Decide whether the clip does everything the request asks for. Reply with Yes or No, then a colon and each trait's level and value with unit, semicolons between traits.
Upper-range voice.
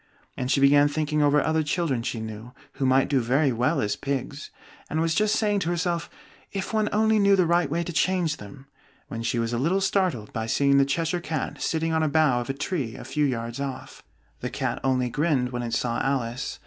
No: medium, 145 Hz